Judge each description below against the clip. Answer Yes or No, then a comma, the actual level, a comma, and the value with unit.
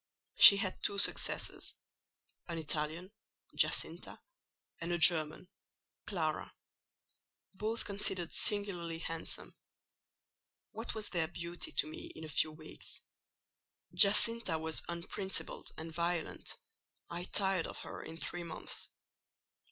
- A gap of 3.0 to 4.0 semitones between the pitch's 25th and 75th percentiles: Yes, average, 3.5 semitones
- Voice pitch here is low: No, medium, 170 Hz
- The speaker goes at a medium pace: No, slow, 115 wpm